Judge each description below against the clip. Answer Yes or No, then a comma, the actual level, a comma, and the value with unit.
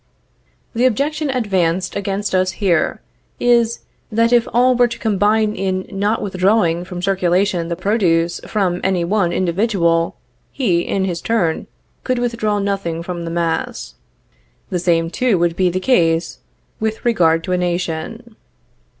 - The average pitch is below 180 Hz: No, high, 190 Hz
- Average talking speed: Yes, average, 145 wpm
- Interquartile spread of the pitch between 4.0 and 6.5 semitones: Yes, average, 4.4 semitones